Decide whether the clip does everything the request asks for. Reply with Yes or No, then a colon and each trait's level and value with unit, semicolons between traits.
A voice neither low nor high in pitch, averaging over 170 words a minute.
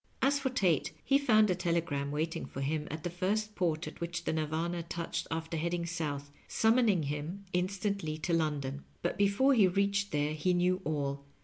Yes: medium, 170 Hz; average, 185 wpm